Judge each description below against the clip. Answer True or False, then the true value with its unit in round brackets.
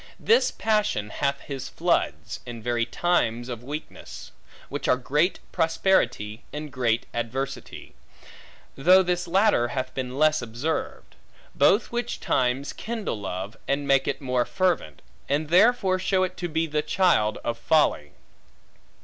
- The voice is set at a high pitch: False (140 Hz)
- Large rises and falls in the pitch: True (6.7 semitones)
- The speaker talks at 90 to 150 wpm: True (140 wpm)